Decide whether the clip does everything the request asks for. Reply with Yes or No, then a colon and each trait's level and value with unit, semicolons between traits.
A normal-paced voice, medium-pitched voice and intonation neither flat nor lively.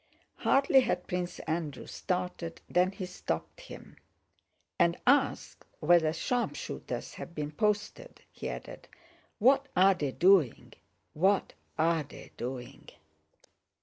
No: slow, 115 wpm; medium, 180 Hz; average, 4.6 semitones